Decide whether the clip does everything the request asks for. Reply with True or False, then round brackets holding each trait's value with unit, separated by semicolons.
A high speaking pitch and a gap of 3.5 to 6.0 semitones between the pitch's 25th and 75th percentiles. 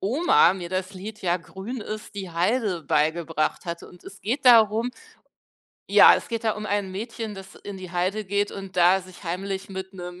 False (195 Hz; 2.9 semitones)